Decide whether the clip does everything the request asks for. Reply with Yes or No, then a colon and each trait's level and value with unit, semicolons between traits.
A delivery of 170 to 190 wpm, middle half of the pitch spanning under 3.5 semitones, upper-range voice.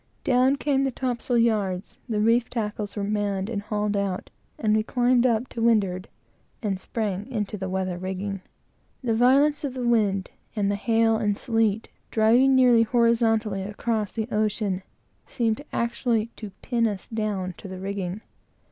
No: average, 160 wpm; average, 2.8 semitones; high, 220 Hz